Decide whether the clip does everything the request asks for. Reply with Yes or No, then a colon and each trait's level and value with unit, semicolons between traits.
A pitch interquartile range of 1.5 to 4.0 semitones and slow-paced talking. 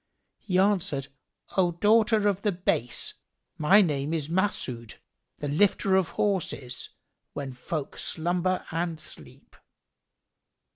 No: average, 5.2 semitones; slow, 110 wpm